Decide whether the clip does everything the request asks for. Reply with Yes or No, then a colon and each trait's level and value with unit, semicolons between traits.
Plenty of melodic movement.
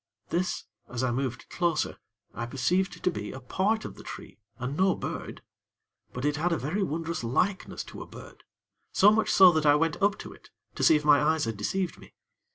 Yes: wide, 5.8 semitones